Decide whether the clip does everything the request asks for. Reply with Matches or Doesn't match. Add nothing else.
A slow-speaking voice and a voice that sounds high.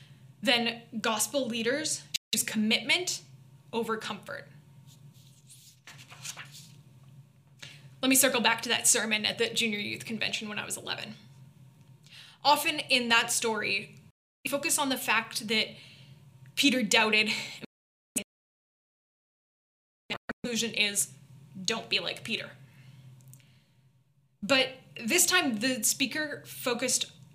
Matches